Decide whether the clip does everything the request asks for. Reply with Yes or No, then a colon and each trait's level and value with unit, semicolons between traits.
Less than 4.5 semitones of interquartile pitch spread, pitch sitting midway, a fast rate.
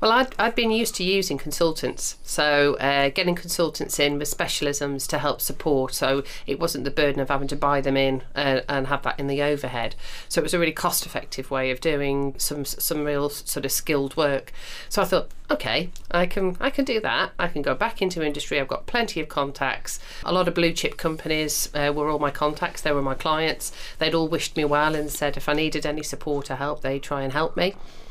Yes: average, 2.8 semitones; medium, 145 Hz; fast, 230 wpm